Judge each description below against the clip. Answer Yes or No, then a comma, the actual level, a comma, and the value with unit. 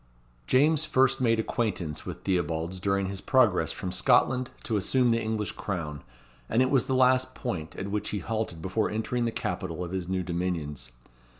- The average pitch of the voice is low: Yes, low, 105 Hz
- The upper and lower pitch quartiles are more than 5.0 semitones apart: Yes, wide, 5.5 semitones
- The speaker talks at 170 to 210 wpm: Yes, average, 180 wpm